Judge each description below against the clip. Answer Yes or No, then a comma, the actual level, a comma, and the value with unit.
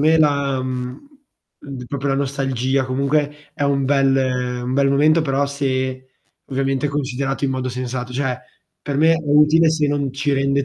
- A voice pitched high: No, medium, 140 Hz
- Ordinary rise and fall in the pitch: No, narrow, 1.8 semitones